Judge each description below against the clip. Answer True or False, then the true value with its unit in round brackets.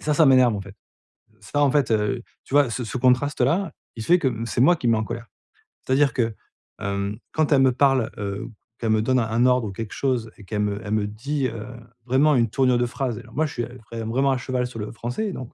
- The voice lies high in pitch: False (125 Hz)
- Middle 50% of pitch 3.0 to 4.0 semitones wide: True (3.3 semitones)